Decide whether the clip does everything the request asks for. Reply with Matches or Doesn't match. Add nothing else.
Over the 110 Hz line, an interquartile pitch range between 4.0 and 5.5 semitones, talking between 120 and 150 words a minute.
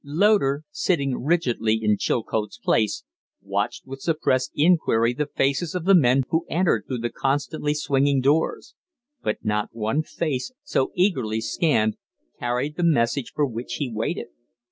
Matches